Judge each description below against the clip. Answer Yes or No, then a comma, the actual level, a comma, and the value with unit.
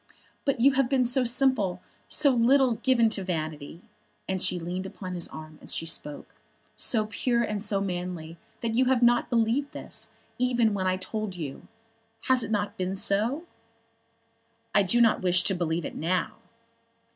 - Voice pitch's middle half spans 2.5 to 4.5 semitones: No, average, 5.0 semitones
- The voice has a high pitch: Yes, high, 210 Hz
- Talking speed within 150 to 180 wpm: Yes, average, 170 wpm